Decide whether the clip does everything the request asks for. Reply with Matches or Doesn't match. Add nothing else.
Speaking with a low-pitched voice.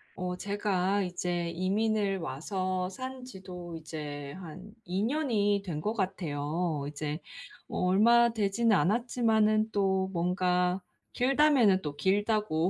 Doesn't match